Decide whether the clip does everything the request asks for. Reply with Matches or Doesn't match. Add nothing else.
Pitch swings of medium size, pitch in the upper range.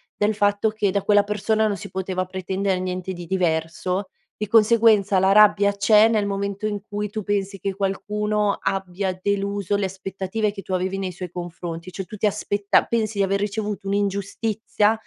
Doesn't match